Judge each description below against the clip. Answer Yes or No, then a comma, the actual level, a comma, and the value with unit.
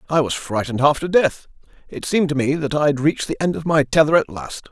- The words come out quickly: Yes, fast, 255 wpm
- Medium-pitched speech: Yes, medium, 145 Hz